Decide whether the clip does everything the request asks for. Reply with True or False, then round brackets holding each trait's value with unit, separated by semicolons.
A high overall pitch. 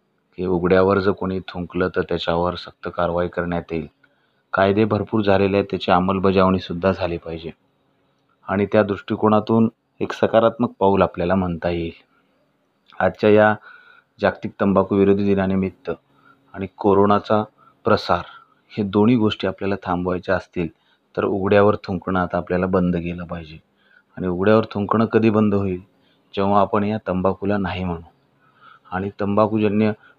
False (95 Hz)